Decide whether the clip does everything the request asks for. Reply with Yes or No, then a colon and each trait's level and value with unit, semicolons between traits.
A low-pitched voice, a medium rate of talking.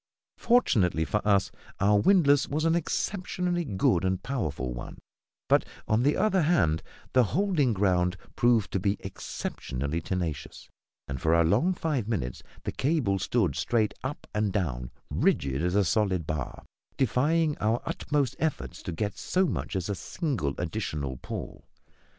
Yes: low, 105 Hz; average, 150 wpm